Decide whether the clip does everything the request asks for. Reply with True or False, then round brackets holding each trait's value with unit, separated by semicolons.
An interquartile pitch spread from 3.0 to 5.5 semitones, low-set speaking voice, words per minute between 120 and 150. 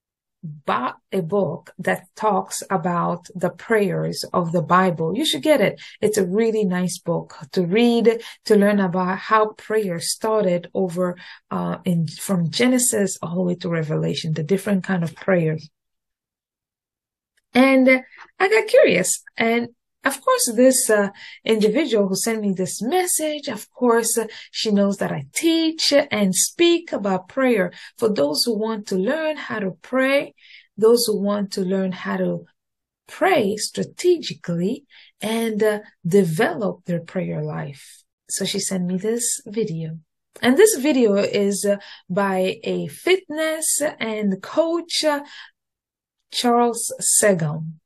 False (5.2 semitones; 205 Hz; 140 wpm)